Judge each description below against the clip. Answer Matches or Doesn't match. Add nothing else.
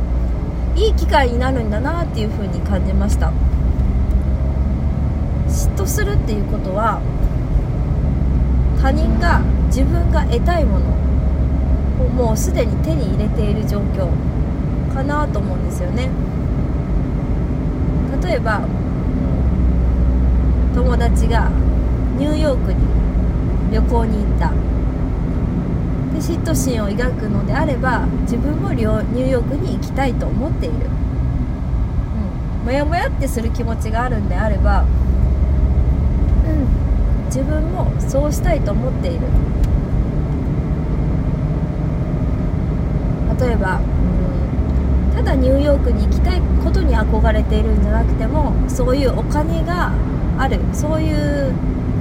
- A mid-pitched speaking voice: Doesn't match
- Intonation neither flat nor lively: Doesn't match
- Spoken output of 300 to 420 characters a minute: Doesn't match